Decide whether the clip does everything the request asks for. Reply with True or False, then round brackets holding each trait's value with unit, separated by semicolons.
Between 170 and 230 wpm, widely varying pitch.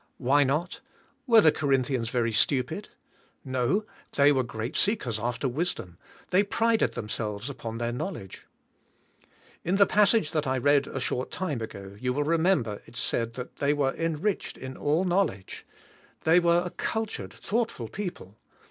False (155 wpm; 6.9 semitones)